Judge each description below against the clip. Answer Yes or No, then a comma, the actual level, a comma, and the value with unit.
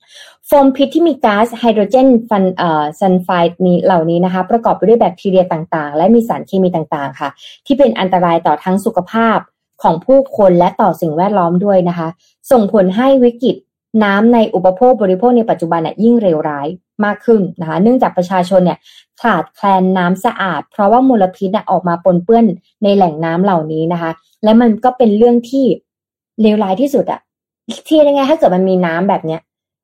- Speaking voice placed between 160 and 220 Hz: Yes, high, 190 Hz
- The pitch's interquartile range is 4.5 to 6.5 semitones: Yes, average, 5.2 semitones